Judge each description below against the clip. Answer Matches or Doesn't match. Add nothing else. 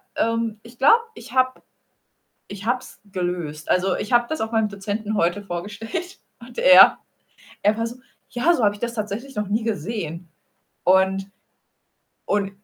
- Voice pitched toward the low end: Doesn't match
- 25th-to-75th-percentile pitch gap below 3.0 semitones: Doesn't match